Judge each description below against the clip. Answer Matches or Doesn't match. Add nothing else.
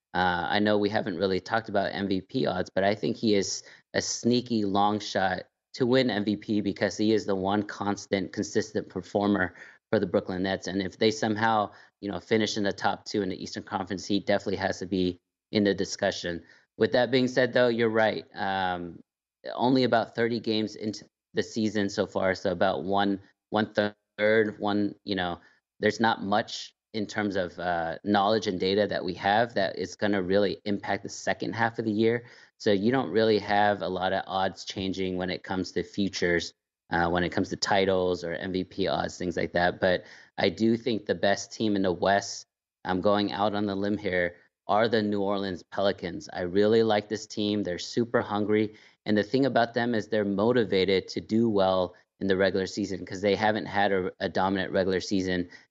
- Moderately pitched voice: Doesn't match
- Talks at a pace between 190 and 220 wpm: Matches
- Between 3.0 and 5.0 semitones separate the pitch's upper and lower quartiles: Doesn't match